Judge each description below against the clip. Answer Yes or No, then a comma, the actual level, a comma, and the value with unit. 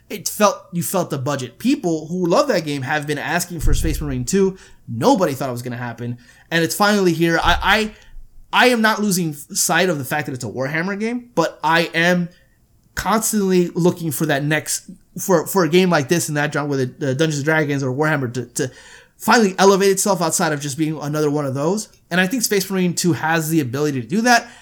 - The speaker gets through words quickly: Yes, fast, 225 wpm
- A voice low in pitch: No, medium, 165 Hz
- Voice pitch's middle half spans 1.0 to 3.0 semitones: No, average, 4.7 semitones